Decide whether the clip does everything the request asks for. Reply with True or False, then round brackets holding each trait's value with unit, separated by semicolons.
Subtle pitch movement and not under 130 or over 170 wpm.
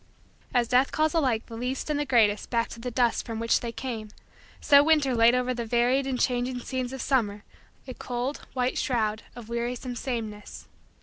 False (2.1 semitones; 190 wpm)